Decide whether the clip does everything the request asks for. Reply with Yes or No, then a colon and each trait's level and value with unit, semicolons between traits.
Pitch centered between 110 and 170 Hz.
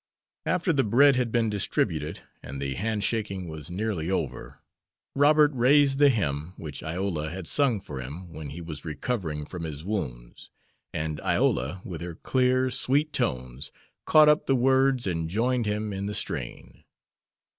No: very low, 95 Hz